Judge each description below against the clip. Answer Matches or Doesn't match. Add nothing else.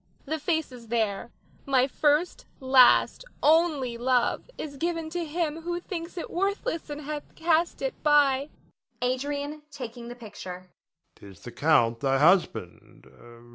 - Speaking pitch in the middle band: Doesn't match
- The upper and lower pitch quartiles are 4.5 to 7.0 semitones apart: Matches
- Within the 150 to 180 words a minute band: Doesn't match